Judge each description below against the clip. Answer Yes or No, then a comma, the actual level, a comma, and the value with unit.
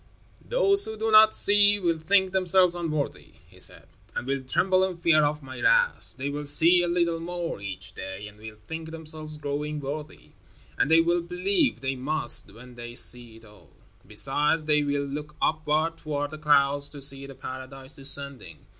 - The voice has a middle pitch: Yes, medium, 150 Hz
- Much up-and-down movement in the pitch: No, average, 4.1 semitones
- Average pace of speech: Yes, average, 180 wpm